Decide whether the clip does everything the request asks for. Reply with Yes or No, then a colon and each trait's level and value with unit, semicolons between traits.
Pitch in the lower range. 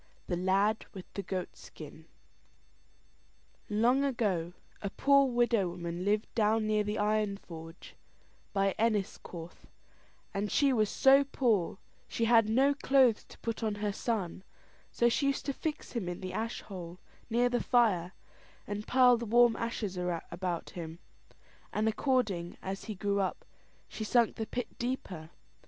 No: high, 215 Hz